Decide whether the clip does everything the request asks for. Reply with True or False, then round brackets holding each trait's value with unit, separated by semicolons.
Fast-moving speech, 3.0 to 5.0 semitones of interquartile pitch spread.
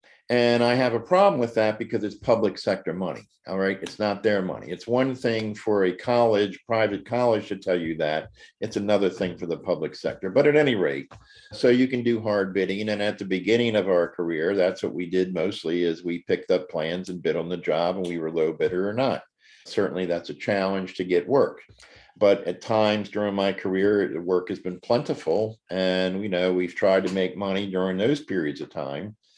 True (220 wpm; 3.8 semitones)